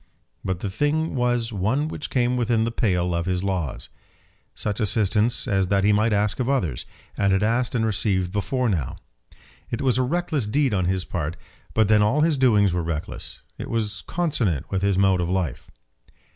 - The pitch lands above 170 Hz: No, low, 105 Hz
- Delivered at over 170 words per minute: Yes, average, 190 wpm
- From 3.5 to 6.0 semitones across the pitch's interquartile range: Yes, average, 4.7 semitones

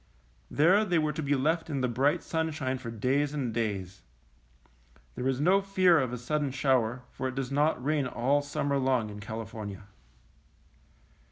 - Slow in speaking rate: No, average, 180 wpm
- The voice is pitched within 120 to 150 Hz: Yes, low, 135 Hz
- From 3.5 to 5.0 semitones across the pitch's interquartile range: Yes, average, 3.8 semitones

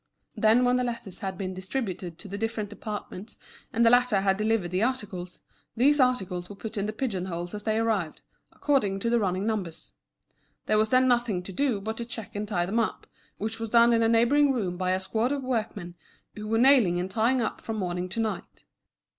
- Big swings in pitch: No, average, 3.7 semitones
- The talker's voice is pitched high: Yes, high, 215 Hz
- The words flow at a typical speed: No, fast, 215 wpm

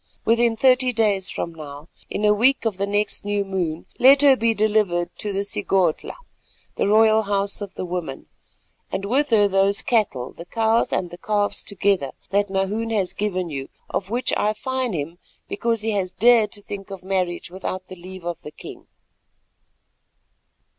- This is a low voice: No, high, 200 Hz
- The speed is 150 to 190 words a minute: Yes, average, 175 wpm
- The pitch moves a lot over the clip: No, average, 3.2 semitones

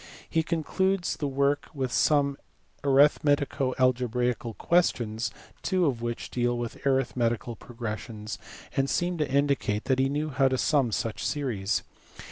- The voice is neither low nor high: No, low, 130 Hz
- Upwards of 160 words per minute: No, slow, 135 wpm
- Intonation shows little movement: No, average, 3.4 semitones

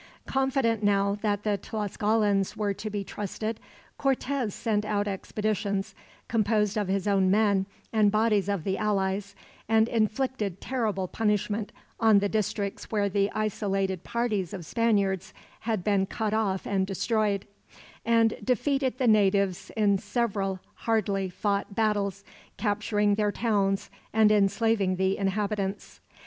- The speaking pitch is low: No, high, 205 Hz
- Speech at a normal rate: No, slow, 130 wpm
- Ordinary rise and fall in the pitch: No, narrow, 2.0 semitones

